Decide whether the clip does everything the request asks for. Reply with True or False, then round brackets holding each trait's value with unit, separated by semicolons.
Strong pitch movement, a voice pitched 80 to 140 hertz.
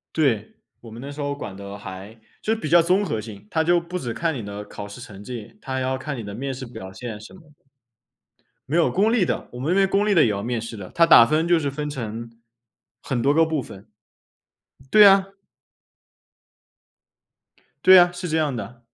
True (7.1 semitones; 135 Hz)